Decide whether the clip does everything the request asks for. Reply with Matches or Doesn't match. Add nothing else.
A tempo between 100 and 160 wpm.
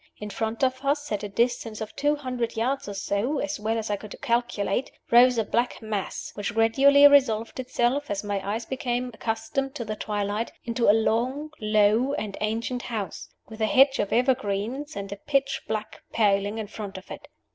Doesn't match